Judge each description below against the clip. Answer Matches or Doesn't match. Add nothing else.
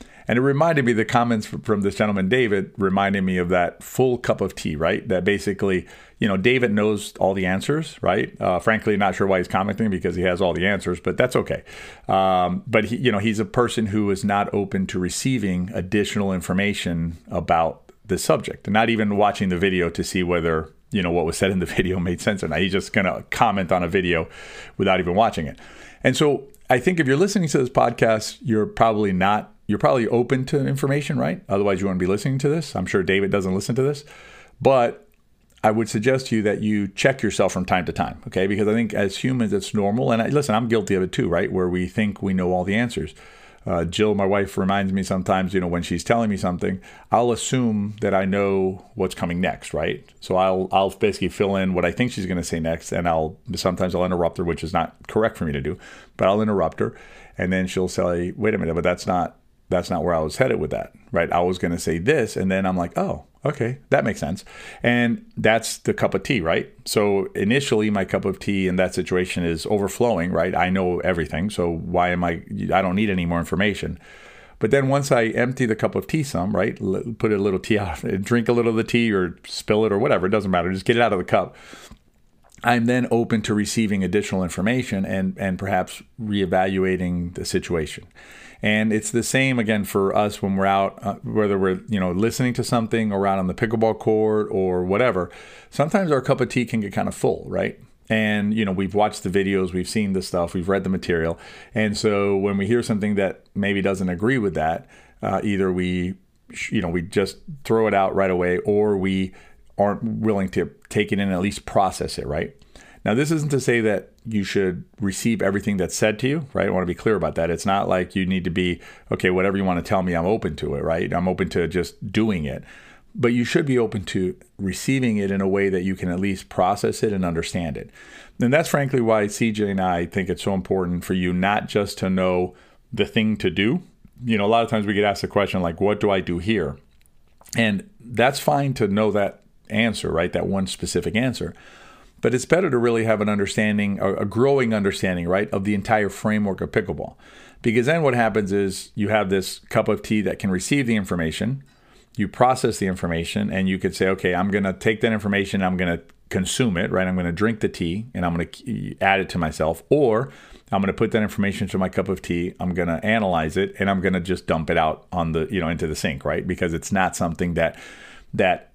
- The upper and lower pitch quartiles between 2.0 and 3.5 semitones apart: Matches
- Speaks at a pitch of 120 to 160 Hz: Doesn't match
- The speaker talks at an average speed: Doesn't match